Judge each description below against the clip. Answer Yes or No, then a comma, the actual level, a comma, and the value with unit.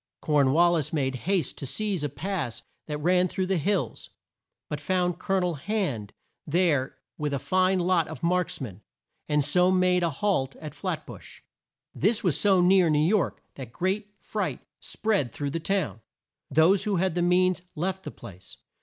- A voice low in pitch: No, medium, 175 Hz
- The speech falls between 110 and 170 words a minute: No, average, 180 wpm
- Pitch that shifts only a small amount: No, average, 4.3 semitones